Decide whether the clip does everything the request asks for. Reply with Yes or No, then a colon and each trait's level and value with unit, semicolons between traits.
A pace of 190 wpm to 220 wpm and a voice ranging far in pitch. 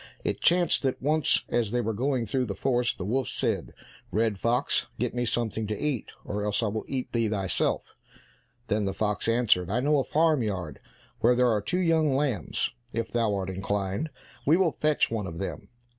No: average, 200 wpm; average, 4.5 semitones